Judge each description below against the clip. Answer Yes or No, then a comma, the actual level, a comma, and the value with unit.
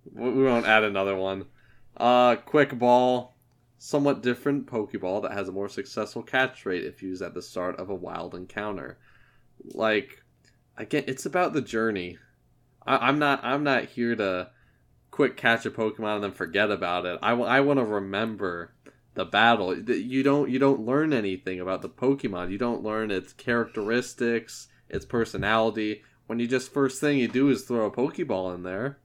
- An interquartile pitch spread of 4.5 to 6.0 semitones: Yes, average, 4.8 semitones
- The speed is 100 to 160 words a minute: No, average, 180 wpm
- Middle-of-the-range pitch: No, low, 120 Hz